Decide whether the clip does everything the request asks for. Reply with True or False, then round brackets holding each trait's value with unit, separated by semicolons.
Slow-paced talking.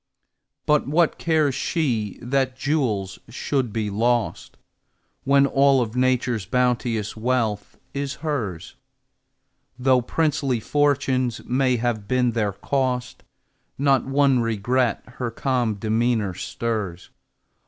True (110 wpm)